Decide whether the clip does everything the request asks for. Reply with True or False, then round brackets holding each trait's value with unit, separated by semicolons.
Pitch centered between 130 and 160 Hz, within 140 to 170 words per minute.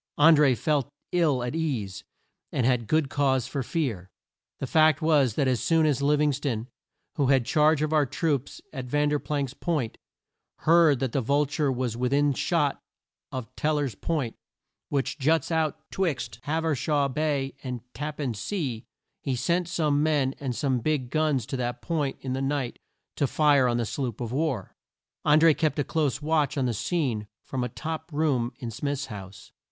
False (140 Hz; 190 wpm)